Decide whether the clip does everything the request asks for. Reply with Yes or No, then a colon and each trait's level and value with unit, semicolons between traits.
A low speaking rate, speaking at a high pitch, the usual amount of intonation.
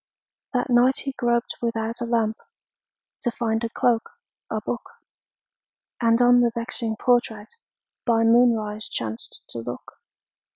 No: slow, 130 wpm; high, 230 Hz; narrow, 1.5 semitones